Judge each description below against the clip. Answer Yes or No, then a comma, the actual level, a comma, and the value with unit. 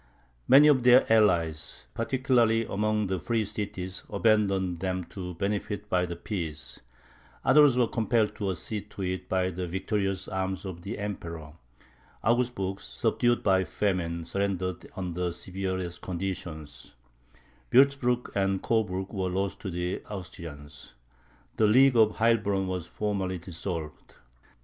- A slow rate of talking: Yes, slow, 130 wpm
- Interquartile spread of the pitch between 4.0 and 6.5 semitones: No, average, 3.2 semitones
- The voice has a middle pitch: No, very low, 95 Hz